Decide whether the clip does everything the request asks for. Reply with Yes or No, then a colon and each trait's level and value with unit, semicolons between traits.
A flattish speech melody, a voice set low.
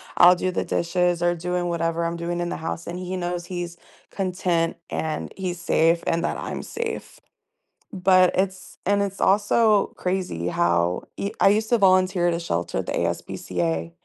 No: narrow, 1.9 semitones; medium, 175 Hz